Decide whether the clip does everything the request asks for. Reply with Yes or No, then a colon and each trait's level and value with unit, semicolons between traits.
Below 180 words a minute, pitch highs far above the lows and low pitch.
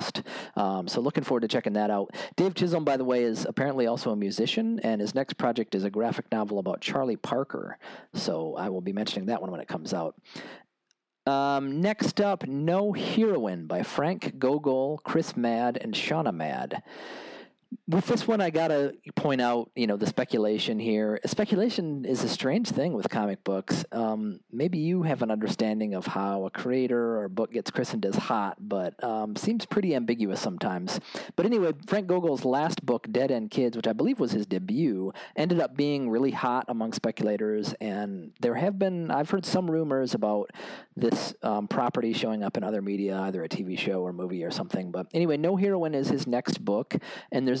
No: average, 195 wpm; wide, 7.4 semitones; low, 125 Hz